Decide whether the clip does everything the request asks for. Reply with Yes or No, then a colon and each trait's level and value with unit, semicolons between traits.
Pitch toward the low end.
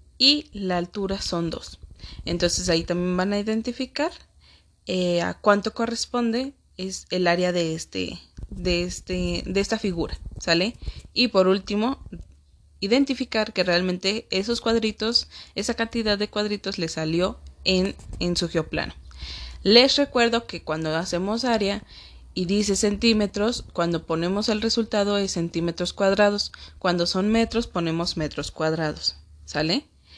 No: medium, 185 Hz